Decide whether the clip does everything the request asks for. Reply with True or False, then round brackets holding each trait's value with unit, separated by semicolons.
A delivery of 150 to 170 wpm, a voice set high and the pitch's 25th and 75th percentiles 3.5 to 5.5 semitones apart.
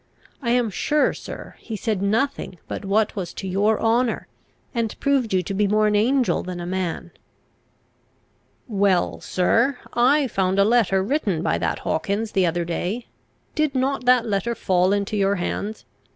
True (165 wpm; 210 Hz; 4.1 semitones)